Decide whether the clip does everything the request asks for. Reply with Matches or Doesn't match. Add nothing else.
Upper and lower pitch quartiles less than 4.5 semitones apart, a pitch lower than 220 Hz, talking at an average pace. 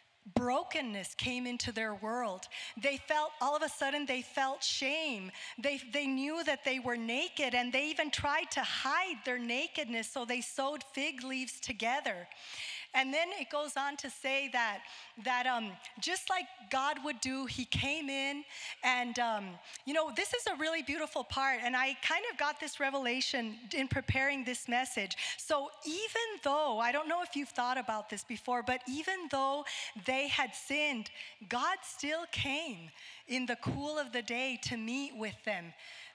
Doesn't match